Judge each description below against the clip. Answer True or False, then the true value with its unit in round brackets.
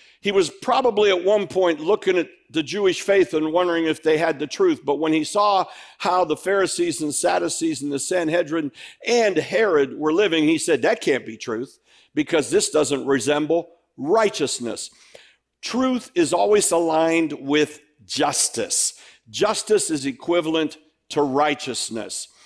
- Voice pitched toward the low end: False (175 Hz)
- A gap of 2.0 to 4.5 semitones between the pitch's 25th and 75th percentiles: False (5.3 semitones)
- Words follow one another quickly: False (150 wpm)